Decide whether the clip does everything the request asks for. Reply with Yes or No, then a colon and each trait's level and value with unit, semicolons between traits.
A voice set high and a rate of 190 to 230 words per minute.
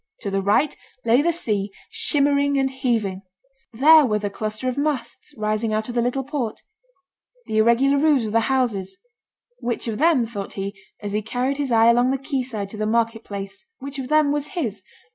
Yes: high, 235 Hz; average, 200 wpm